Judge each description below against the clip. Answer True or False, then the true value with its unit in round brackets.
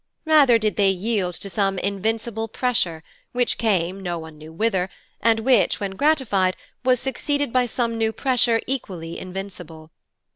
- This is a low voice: False (215 Hz)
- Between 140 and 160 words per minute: True (150 wpm)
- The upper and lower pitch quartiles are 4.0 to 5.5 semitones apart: True (4.7 semitones)